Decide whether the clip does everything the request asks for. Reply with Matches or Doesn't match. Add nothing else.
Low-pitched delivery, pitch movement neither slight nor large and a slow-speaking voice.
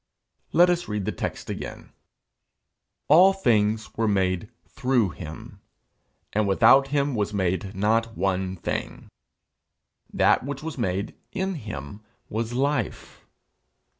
Doesn't match